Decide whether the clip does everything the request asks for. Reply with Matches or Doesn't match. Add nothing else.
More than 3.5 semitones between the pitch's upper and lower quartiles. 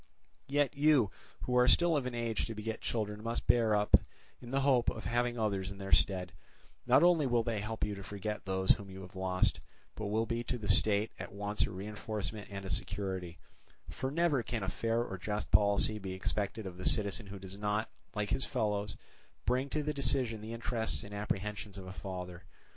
Doesn't match